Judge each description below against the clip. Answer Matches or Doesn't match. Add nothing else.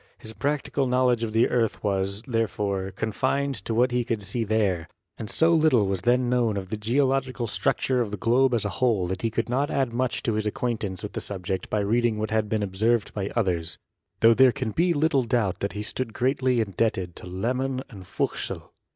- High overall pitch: Doesn't match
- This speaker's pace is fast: Matches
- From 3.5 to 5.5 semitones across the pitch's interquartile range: Matches